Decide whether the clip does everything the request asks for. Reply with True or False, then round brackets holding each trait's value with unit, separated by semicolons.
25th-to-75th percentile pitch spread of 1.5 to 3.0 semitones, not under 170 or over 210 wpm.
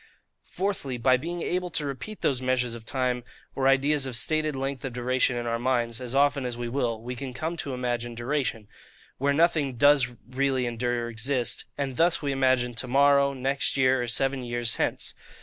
True (2.5 semitones; 190 wpm)